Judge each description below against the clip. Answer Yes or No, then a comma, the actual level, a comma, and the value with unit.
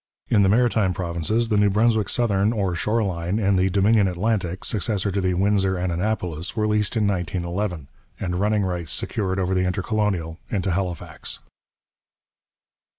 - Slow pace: No, average, 155 wpm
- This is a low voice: Yes, very low, 95 Hz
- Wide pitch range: No, average, 2.9 semitones